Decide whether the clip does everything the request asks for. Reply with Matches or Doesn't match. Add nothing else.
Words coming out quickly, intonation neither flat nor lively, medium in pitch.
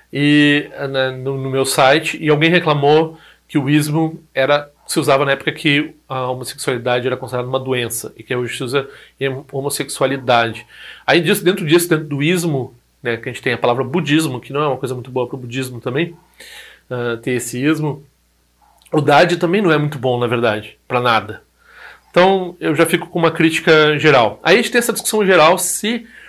Matches